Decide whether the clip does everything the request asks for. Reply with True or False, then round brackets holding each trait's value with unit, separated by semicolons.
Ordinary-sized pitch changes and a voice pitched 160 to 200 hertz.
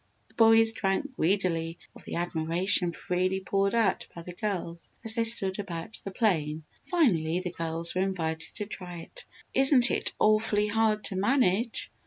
True (4.6 semitones; 190 Hz)